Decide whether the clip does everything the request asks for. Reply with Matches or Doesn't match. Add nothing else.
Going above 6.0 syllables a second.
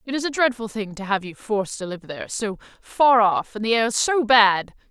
Doesn't match